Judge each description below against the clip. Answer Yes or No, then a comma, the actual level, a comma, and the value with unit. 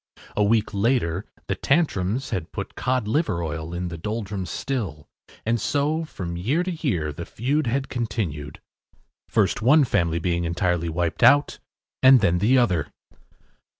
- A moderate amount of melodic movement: No, wide, 7.2 semitones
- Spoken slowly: No, average, 150 wpm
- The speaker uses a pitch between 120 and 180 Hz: No, low, 105 Hz